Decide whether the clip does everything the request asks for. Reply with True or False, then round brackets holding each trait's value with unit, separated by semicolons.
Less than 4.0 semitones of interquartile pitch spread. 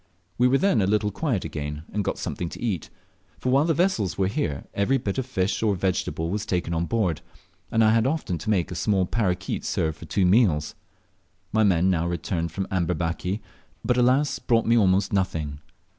False (4.9 semitones)